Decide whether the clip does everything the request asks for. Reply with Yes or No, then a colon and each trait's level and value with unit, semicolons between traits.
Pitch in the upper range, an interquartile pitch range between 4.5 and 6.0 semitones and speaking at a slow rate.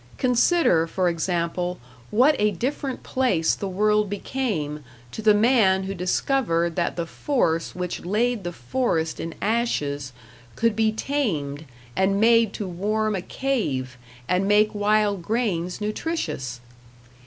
Yes: high, 200 Hz; average, 5.2 semitones; slow, 130 wpm